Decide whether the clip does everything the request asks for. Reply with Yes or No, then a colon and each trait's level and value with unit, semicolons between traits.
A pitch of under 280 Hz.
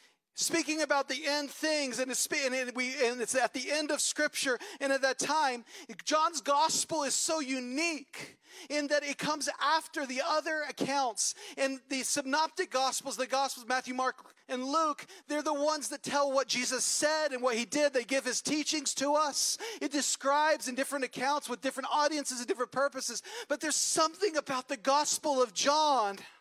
No: very high, 285 Hz